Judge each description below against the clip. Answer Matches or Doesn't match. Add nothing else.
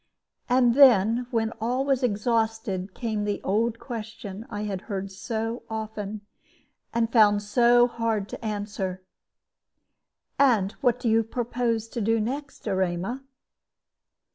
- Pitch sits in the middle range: Doesn't match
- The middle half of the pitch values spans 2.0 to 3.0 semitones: Matches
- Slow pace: Matches